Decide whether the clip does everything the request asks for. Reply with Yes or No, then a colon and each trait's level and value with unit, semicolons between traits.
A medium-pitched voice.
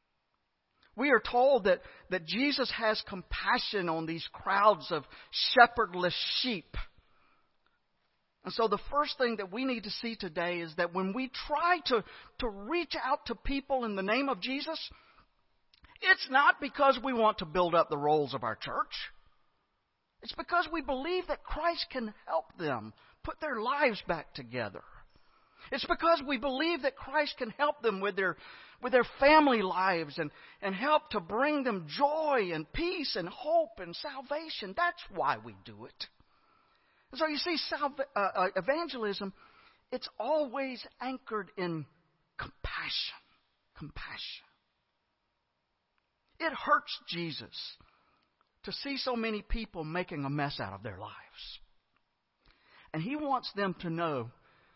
No: high, 240 Hz